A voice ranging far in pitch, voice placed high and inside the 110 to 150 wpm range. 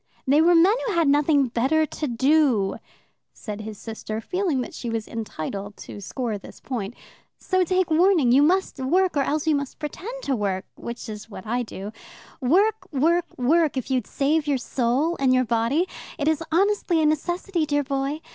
No: wide, 5.8 semitones; very high, 280 Hz; average, 185 wpm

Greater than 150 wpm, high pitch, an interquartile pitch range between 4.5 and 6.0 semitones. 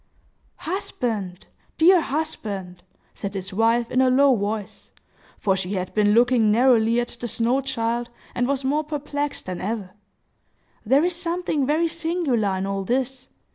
No: average, 140 wpm; high, 240 Hz; wide, 5.5 semitones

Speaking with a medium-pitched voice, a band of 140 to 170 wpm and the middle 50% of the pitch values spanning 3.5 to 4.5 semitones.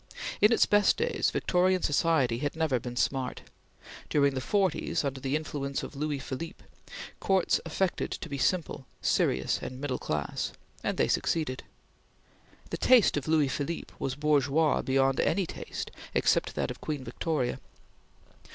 Yes: medium, 145 Hz; average, 150 wpm; average, 3.8 semitones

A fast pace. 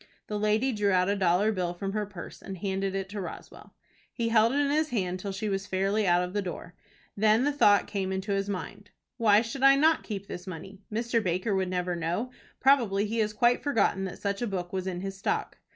Yes: fast, 230 wpm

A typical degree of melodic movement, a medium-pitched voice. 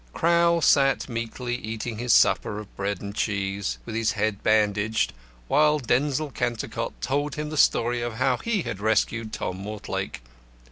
No: average, 4.4 semitones; low, 115 Hz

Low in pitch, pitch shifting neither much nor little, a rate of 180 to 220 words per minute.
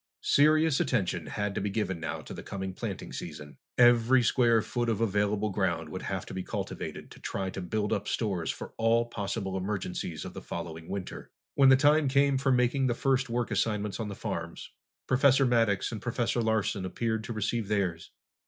Yes: low, 110 Hz; average, 4.2 semitones; average, 190 wpm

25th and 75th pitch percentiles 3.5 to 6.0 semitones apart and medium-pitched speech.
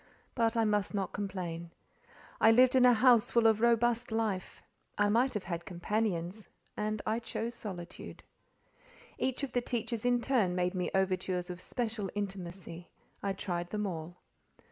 No: average, 4.2 semitones; high, 210 Hz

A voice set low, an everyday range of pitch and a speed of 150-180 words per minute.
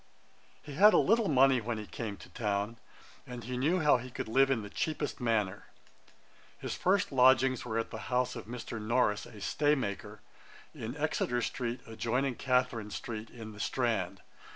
Yes: low, 120 Hz; average, 3.3 semitones; average, 175 wpm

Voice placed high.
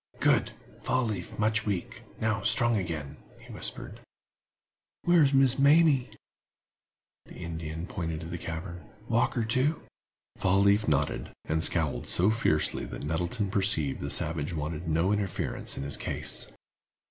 No: very low, 95 Hz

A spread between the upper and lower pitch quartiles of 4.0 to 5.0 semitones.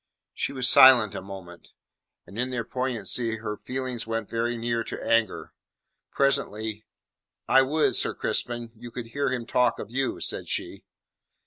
No: narrow, 2.5 semitones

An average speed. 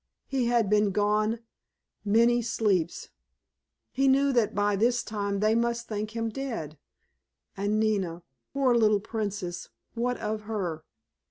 No: slow, 120 wpm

